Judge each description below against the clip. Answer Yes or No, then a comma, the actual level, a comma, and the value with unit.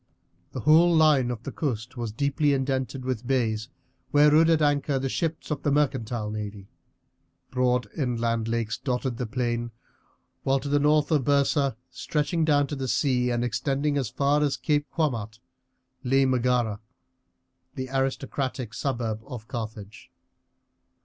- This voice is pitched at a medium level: No, low, 130 Hz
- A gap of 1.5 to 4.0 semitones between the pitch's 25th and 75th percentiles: Yes, average, 3.6 semitones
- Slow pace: No, average, 150 wpm